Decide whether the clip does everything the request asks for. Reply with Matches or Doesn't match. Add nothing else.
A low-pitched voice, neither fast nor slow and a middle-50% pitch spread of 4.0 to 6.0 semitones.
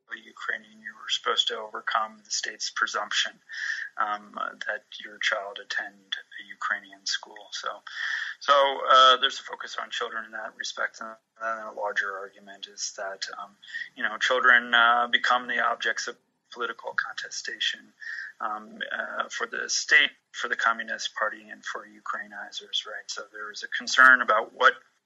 Matches